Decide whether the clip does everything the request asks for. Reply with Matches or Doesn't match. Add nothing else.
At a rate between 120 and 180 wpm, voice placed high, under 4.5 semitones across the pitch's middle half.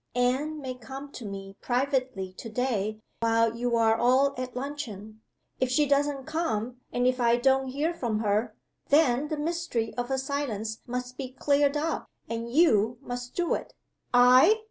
Matches